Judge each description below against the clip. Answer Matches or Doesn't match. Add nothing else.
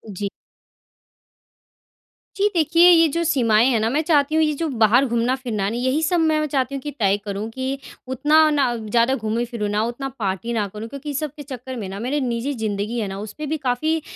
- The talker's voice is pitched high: Matches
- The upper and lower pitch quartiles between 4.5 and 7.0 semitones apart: Matches